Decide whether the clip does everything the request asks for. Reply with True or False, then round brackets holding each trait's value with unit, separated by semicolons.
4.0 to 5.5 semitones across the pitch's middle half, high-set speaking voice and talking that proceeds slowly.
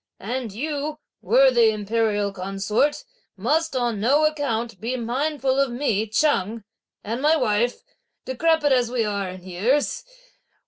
True (5.2 semitones; 240 Hz; 130 wpm)